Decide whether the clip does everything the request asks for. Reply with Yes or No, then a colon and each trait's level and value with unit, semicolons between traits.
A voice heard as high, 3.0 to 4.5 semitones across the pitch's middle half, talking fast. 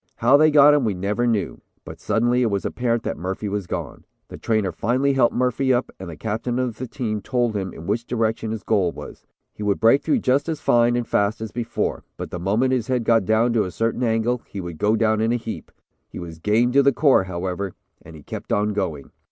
No: low, 115 Hz; average, 3.4 semitones; fast, 240 wpm